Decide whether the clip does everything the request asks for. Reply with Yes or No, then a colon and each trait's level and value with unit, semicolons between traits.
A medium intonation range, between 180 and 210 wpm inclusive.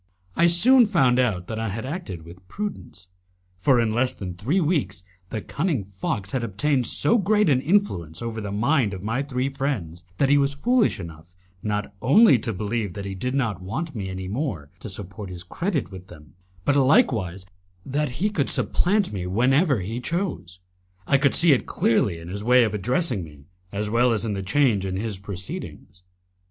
No: wide, 6.9 semitones; average, 190 wpm